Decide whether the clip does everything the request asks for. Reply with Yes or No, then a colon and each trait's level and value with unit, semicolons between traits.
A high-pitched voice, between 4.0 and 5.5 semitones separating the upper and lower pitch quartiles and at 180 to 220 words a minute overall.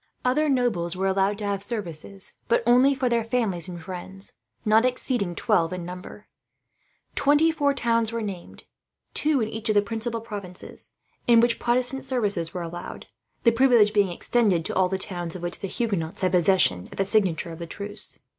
Yes: high, 205 Hz; average, 4.7 semitones; average, 185 wpm